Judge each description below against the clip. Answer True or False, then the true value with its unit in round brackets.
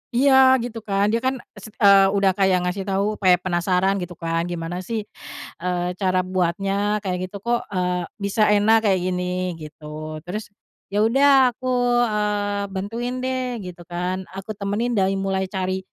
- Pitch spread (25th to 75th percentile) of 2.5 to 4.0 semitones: True (3.5 semitones)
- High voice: True (195 Hz)